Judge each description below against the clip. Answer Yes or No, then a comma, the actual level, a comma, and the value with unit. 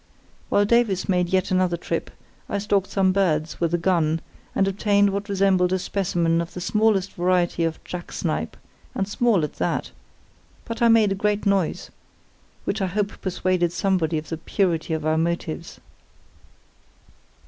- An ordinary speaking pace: Yes, average, 160 wpm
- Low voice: No, medium, 185 Hz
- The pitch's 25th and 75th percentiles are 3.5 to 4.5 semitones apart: No, average, 2.7 semitones